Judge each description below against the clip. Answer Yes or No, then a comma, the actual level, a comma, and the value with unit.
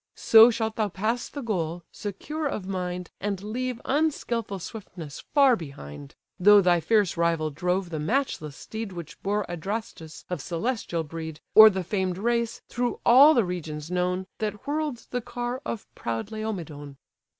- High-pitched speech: Yes, high, 195 Hz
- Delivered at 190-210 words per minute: No, average, 155 wpm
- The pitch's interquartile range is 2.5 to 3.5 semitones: No, average, 5.3 semitones